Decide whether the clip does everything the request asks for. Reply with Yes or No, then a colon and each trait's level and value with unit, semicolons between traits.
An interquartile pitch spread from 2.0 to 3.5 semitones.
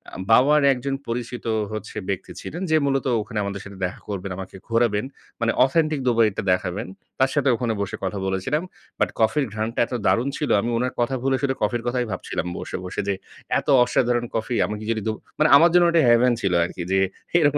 No: average, 4.7 semitones